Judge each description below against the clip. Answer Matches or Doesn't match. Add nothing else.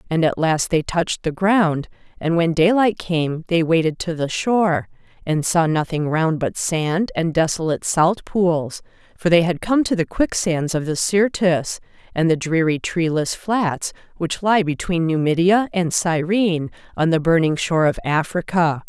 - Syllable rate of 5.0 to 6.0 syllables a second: Doesn't match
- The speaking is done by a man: Doesn't match